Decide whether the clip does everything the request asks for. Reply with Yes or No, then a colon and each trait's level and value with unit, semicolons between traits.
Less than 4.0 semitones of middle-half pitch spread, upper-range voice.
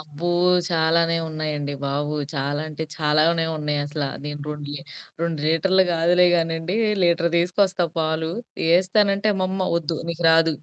No: narrow, 2.5 semitones; medium, 165 Hz